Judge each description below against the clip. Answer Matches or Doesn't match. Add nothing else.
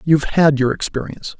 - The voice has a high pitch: Doesn't match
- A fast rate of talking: Doesn't match